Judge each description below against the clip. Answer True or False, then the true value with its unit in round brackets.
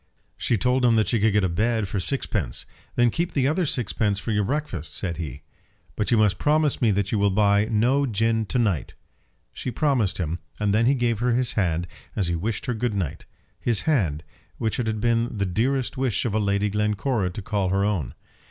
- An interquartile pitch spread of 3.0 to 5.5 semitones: True (3.7 semitones)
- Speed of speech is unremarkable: False (215 wpm)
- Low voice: True (110 Hz)